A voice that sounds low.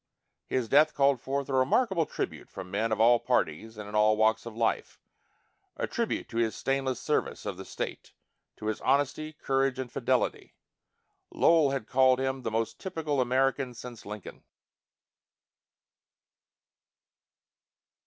Yes: low, 130 Hz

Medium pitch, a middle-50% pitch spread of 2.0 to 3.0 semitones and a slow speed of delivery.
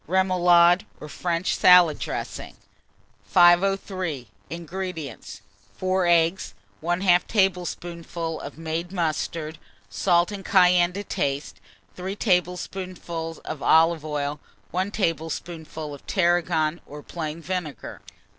Yes: medium, 175 Hz; narrow, 2.4 semitones; slow, 100 wpm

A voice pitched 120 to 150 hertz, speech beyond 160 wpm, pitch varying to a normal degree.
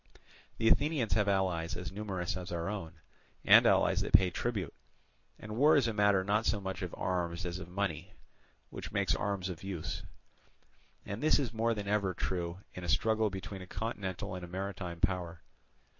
No: very low, 95 Hz; average, 185 wpm; average, 3.0 semitones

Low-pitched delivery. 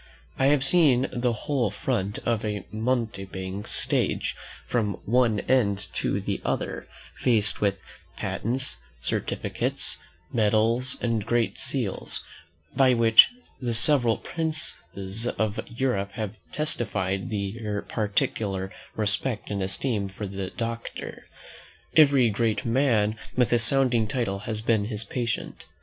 Yes: low, 115 Hz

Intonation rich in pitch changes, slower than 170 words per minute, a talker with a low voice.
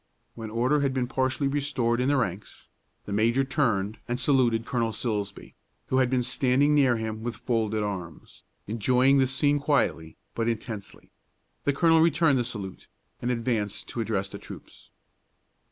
No: average, 3.6 semitones; average, 160 wpm; low, 120 Hz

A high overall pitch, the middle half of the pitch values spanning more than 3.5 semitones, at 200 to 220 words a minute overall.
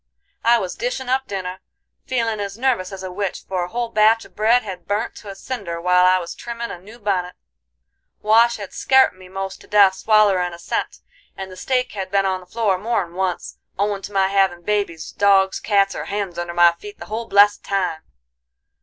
No: high, 195 Hz; average, 2.9 semitones; fast, 205 wpm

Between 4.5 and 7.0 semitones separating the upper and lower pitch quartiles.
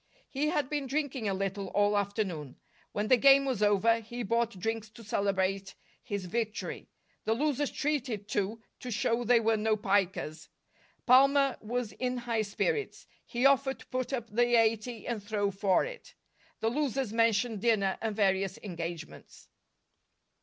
No: average, 3.8 semitones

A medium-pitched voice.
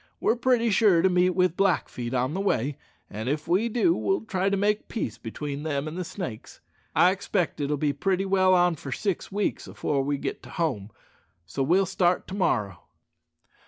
Yes: medium, 180 Hz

